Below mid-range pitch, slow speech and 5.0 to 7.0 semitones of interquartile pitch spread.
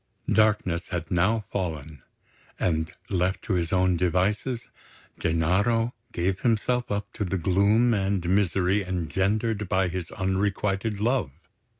No: very low, 95 Hz; slow, 120 wpm; average, 3.0 semitones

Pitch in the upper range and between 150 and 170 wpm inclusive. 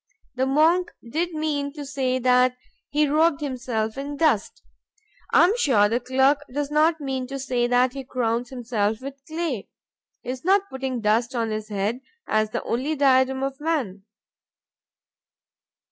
Yes: very high, 265 Hz; average, 160 wpm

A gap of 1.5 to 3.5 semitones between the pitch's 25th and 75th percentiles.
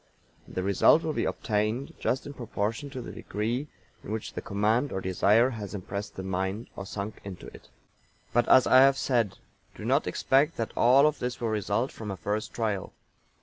No: average, 4.3 semitones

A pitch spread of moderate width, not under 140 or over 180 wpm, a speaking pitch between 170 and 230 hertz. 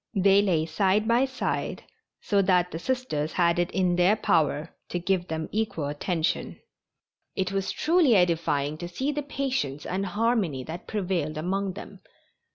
Yes: average, 4.3 semitones; average, 160 wpm; medium, 185 Hz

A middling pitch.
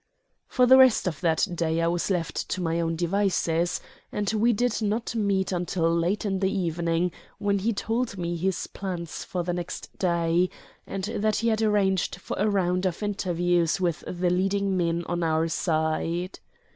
Yes: medium, 180 Hz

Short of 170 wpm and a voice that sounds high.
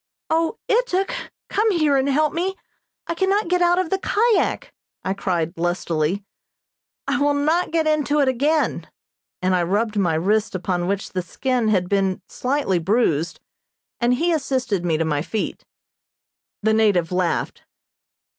Yes: average, 155 wpm; high, 240 Hz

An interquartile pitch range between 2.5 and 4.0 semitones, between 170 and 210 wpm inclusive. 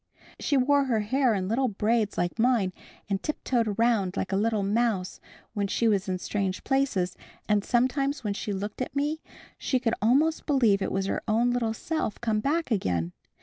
No: average, 4.4 semitones; average, 190 wpm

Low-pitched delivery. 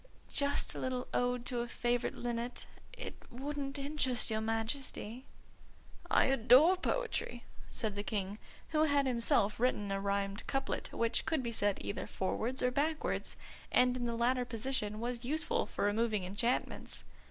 No: high, 245 Hz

